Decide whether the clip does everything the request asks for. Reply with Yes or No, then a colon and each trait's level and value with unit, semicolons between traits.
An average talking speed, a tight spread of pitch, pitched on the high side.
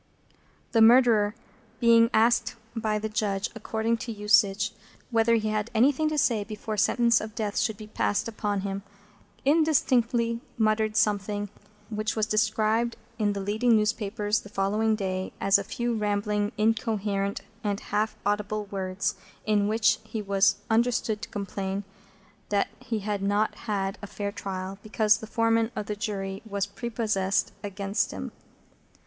Yes: average, 150 wpm; narrow, 1.8 semitones; high, 215 Hz